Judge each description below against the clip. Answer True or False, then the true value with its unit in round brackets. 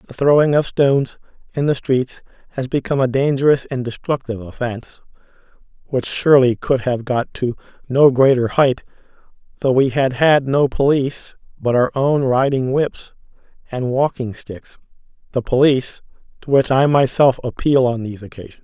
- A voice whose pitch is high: False (130 Hz)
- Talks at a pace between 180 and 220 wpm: False (150 wpm)